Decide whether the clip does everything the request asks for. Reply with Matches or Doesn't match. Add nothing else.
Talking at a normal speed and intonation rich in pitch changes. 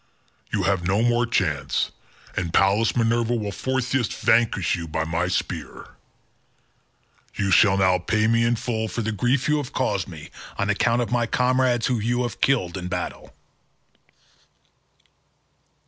Doesn't match